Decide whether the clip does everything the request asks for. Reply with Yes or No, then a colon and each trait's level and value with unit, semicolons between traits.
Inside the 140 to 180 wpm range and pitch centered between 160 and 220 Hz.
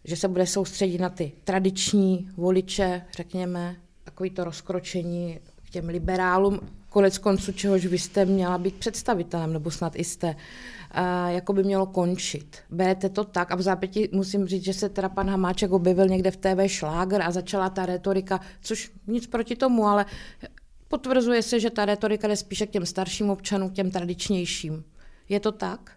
Yes: fast, 170 wpm; high, 190 Hz